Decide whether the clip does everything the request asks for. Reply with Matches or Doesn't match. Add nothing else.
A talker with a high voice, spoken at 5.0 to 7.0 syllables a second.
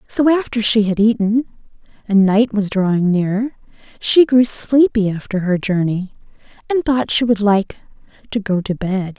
Doesn't match